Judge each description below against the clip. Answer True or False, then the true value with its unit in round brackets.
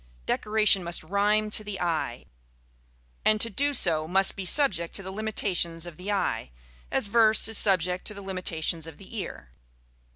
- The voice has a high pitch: True (195 Hz)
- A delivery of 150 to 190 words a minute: True (170 wpm)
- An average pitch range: True (3.7 semitones)